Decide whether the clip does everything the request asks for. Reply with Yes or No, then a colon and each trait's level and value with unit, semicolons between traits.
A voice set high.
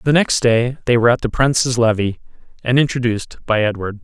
No: low, 120 Hz